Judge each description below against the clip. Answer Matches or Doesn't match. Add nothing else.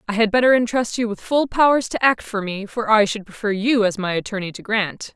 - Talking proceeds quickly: Matches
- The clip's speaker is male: Doesn't match